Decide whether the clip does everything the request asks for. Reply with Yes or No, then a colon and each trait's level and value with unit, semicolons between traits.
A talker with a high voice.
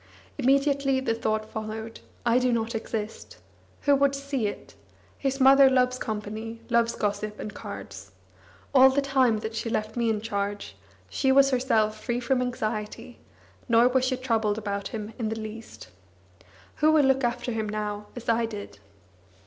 Yes: high, 230 Hz